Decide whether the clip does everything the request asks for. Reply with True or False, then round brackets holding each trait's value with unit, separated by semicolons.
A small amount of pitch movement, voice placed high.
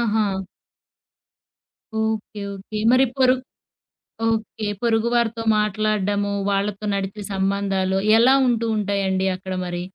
True (2.3 semitones; 210 Hz)